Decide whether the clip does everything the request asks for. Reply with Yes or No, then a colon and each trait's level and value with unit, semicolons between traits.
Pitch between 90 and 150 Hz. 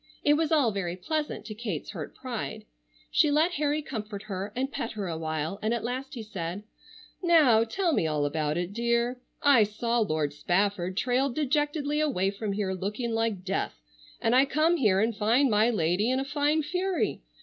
No: high, 230 Hz